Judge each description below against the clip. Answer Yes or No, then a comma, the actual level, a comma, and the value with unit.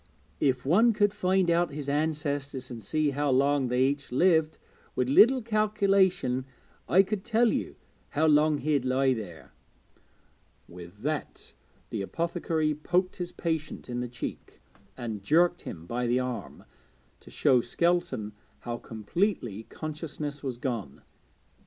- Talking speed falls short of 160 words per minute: Yes, average, 140 wpm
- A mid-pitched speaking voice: Yes, medium, 145 Hz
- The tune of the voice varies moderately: No, wide, 5.8 semitones